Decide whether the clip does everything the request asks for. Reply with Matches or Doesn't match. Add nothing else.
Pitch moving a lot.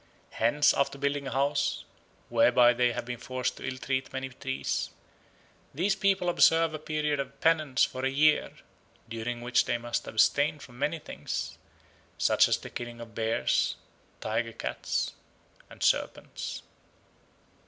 Doesn't match